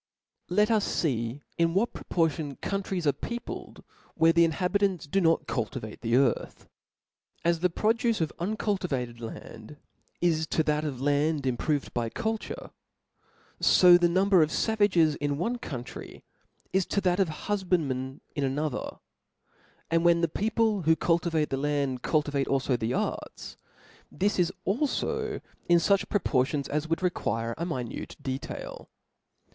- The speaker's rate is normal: Yes, average, 150 wpm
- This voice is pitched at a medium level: Yes, medium, 165 Hz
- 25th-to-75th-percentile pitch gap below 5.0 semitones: No, average, 5.3 semitones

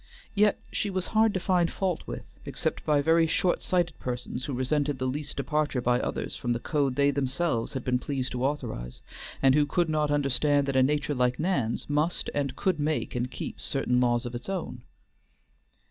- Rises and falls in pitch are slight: No, average, 3.9 semitones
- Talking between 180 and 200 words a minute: Yes, average, 190 wpm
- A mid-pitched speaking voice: Yes, medium, 145 Hz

